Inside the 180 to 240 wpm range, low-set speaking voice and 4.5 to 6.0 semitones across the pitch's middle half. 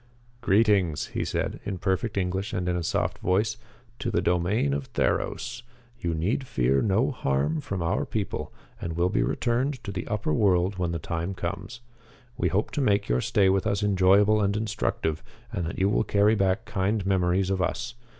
No: average, 190 wpm; very low, 95 Hz; average, 3.2 semitones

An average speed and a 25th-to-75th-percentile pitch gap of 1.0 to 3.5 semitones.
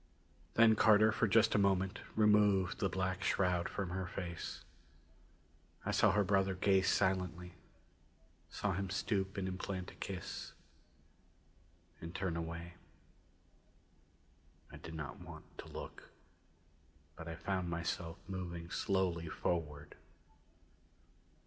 No: slow, 115 wpm; narrow, 2.4 semitones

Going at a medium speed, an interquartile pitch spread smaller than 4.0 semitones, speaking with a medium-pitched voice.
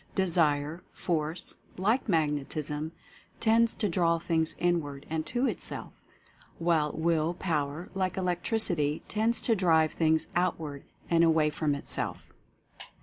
No: slow, 120 wpm; average, 3.1 semitones; medium, 165 Hz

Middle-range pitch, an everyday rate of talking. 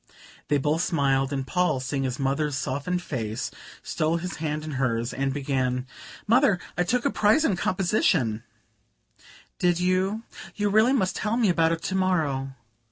Yes: medium, 160 Hz; average, 165 wpm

